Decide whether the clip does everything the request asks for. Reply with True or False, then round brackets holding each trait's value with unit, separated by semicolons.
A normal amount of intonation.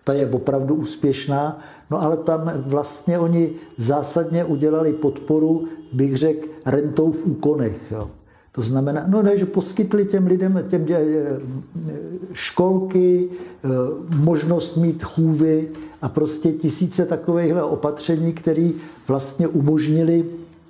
False (2.3 semitones)